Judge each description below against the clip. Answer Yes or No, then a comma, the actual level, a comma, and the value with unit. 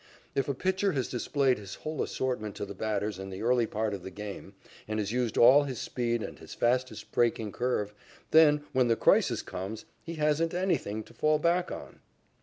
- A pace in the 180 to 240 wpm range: Yes, average, 200 wpm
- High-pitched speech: No, low, 120 Hz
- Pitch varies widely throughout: Yes, wide, 5.7 semitones